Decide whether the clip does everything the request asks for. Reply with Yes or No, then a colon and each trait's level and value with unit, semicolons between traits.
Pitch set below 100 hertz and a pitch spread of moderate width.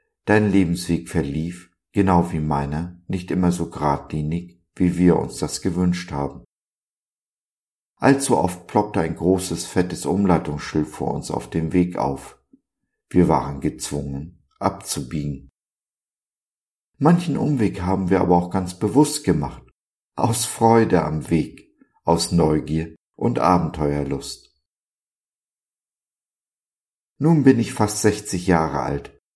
Yes: very low, 90 Hz; average, 4.0 semitones